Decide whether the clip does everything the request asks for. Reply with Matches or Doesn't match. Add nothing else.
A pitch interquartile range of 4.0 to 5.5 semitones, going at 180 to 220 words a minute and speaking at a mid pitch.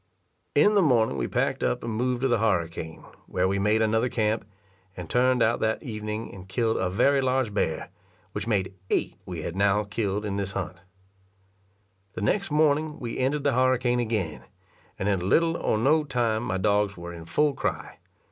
Doesn't match